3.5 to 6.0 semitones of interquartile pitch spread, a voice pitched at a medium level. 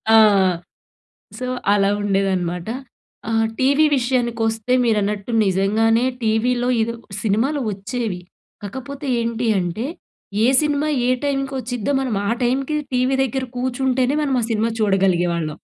No: average, 4.2 semitones; high, 230 Hz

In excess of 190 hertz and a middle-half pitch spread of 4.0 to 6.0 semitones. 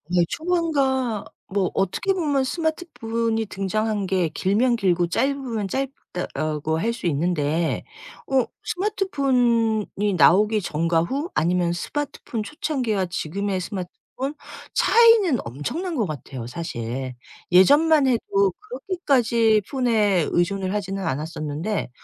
No: high, 215 Hz; wide, 7.4 semitones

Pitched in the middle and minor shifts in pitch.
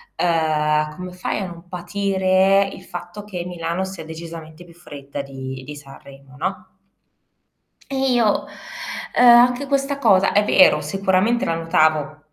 No: medium, 175 Hz; average, 4.2 semitones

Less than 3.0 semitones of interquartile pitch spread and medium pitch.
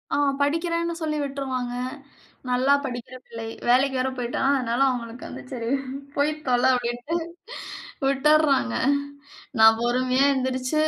No: narrow, 2.6 semitones; very high, 255 Hz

